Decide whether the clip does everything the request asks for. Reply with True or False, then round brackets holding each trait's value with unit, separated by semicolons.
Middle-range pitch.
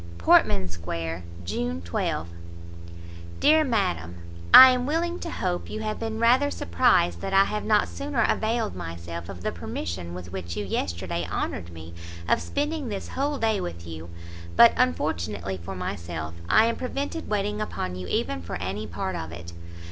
False (95 Hz)